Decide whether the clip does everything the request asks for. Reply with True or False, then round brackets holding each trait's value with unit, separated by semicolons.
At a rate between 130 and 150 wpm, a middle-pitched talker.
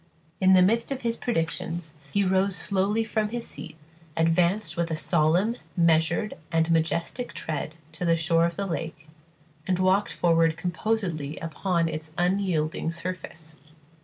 True (145 wpm; 170 Hz)